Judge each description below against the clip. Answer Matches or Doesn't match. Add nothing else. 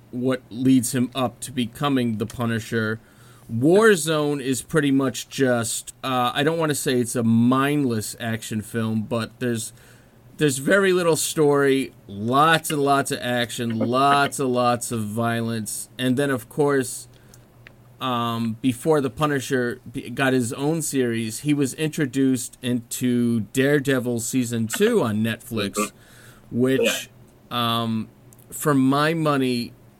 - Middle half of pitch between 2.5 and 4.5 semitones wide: Matches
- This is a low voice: Matches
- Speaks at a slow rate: Matches